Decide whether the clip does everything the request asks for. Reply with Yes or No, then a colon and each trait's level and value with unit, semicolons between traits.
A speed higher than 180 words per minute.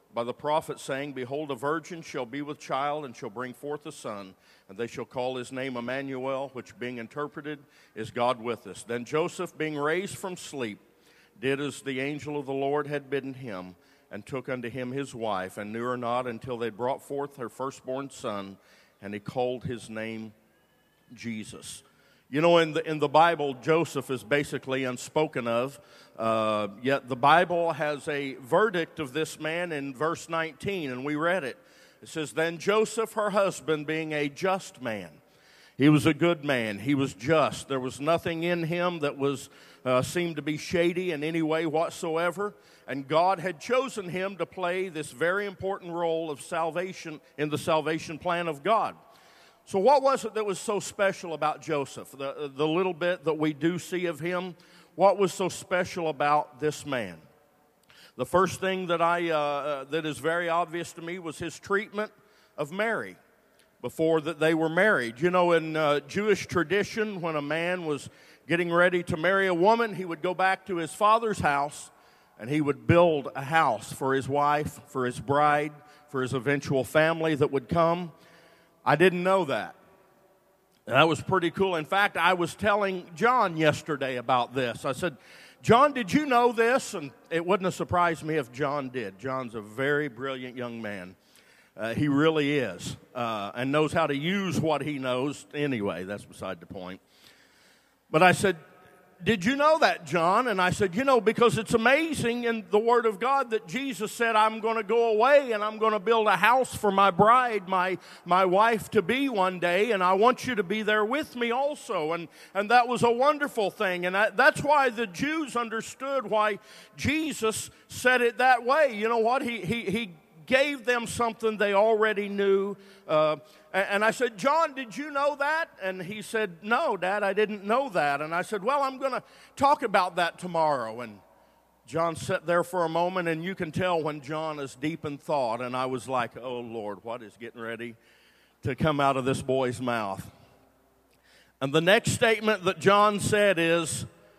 Yes: average, 190 wpm